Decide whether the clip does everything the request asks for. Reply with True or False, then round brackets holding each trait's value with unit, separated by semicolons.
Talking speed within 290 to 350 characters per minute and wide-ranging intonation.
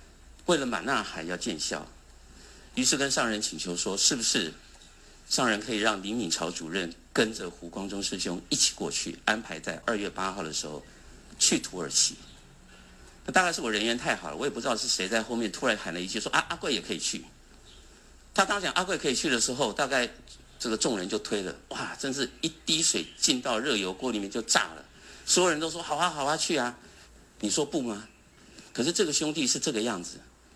True (295 characters per minute; 7.8 semitones)